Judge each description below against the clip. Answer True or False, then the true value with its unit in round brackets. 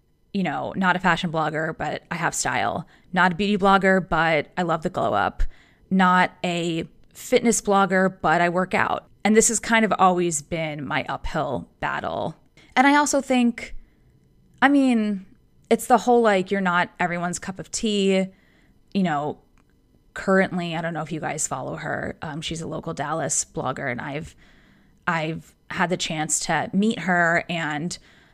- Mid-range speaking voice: True (180 Hz)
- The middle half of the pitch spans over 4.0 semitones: False (3.6 semitones)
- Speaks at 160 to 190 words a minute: True (170 wpm)